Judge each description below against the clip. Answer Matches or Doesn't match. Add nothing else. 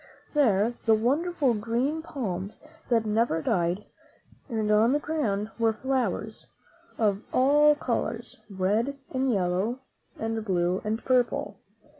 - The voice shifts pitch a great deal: Doesn't match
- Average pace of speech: Doesn't match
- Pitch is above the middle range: Matches